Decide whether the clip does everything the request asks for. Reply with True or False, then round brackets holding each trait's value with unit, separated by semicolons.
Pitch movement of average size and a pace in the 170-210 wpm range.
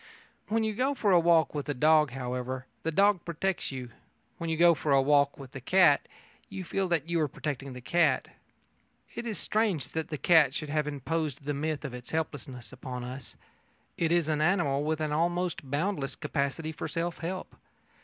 True (3.7 semitones; 195 wpm)